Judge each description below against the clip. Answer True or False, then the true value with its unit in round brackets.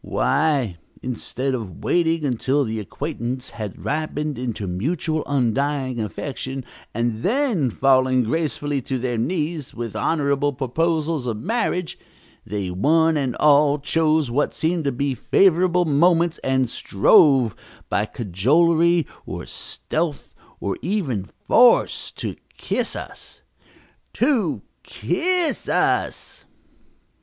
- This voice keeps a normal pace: False (110 wpm)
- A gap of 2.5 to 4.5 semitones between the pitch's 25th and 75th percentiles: False (5.1 semitones)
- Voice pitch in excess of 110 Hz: True (140 Hz)